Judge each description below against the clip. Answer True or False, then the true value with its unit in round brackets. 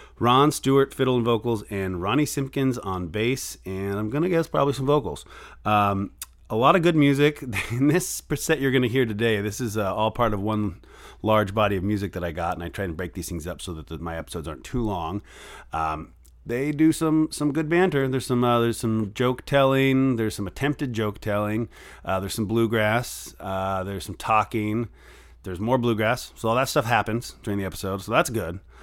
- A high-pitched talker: False (110 Hz)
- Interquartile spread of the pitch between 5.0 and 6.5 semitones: True (5.4 semitones)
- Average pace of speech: False (210 wpm)